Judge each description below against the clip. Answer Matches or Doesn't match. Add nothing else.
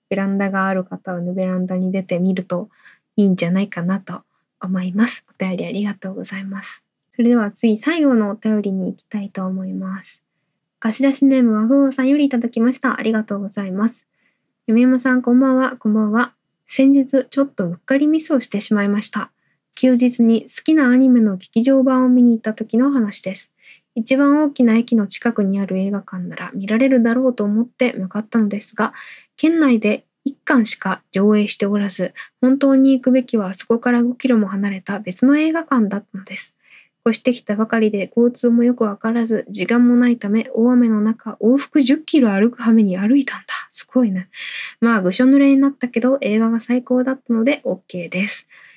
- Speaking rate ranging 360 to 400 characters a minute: Matches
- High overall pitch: Matches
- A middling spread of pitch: Matches